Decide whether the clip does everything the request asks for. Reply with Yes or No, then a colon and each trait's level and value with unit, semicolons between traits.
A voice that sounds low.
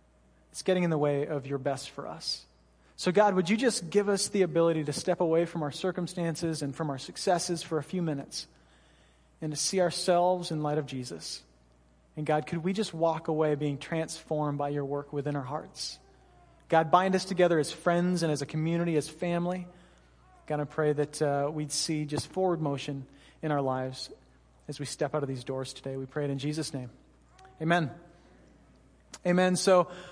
No: medium, 150 Hz